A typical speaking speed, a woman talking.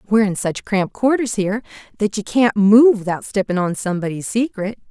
Yes: average, 185 wpm; female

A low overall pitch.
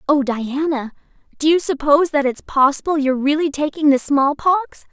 No: very high, 290 Hz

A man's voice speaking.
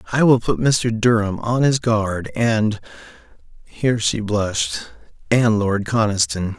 Yes: male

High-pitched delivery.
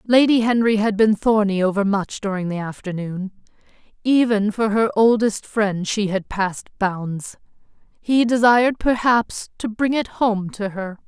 Yes: high, 210 Hz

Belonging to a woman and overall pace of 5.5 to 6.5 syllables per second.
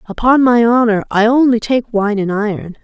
No: female; 5.0 syllables/s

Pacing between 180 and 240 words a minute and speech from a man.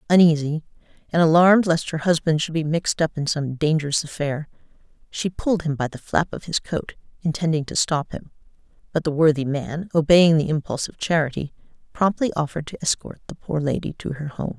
No: average, 190 wpm; female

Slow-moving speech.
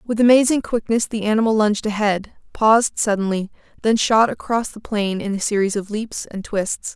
No: average, 180 wpm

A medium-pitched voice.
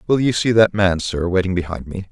No: low, 100 Hz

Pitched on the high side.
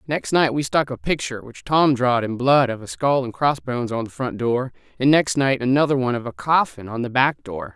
No: low, 130 Hz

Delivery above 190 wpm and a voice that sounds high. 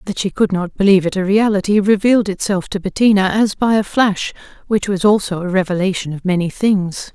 Yes: average, 200 wpm; high, 195 Hz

